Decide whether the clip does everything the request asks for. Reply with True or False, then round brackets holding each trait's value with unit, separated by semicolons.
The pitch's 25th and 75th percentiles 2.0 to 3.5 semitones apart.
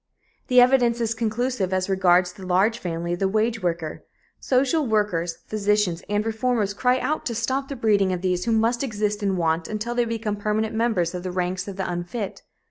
False (4.2 semitones)